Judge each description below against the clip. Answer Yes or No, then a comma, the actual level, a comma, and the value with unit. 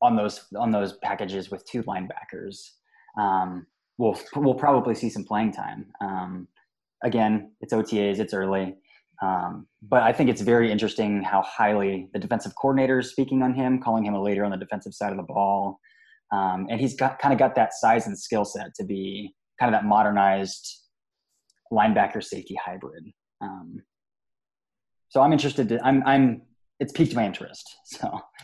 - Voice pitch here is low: Yes, low, 115 Hz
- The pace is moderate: Yes, average, 175 wpm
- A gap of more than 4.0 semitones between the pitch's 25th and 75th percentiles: Yes, average, 5.1 semitones